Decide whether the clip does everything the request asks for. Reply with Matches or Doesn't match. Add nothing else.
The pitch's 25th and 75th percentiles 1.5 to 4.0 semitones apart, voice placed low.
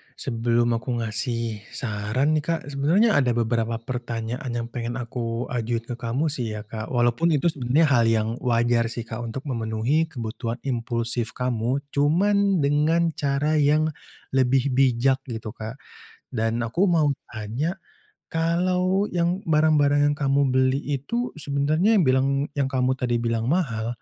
Doesn't match